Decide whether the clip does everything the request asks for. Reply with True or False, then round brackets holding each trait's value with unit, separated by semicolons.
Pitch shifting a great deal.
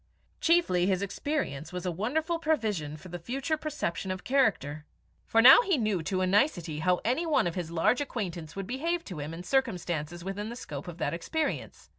True (8.0 semitones)